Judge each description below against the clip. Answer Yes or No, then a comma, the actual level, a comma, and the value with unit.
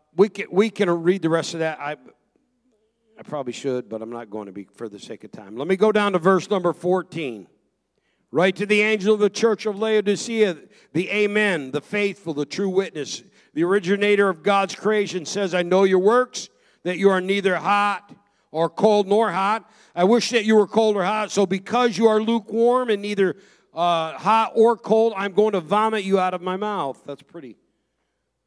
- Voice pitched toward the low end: No, high, 200 Hz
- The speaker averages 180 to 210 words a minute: Yes, fast, 205 wpm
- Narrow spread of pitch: No, average, 3.1 semitones